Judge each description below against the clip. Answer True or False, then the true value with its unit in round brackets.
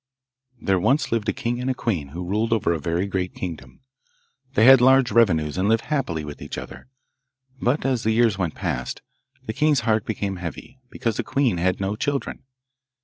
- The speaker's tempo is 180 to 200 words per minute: True (195 wpm)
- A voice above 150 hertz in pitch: False (110 Hz)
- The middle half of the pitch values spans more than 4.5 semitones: True (5.6 semitones)